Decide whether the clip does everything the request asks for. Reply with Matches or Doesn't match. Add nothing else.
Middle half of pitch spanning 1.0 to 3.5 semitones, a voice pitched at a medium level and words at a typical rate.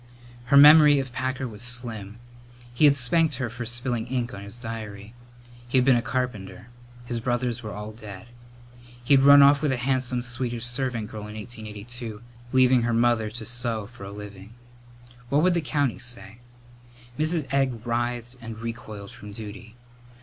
Doesn't match